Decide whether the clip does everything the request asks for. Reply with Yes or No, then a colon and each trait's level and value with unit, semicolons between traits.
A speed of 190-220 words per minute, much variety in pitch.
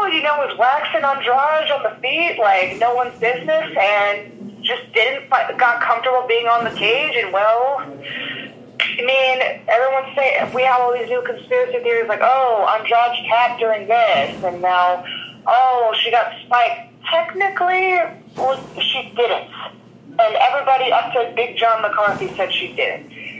No: average, 160 wpm; wide, 5.8 semitones